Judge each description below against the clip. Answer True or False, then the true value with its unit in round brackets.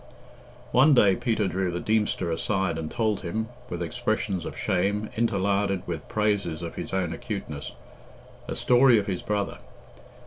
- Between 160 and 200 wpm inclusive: False (150 wpm)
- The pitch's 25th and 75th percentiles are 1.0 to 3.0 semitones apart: False (3.5 semitones)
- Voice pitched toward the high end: False (100 Hz)